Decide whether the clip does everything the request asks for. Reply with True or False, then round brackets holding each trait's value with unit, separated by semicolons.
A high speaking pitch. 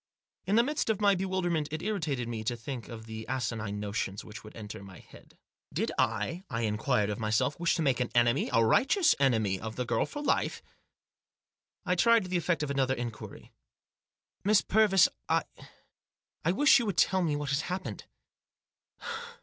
False (135 Hz)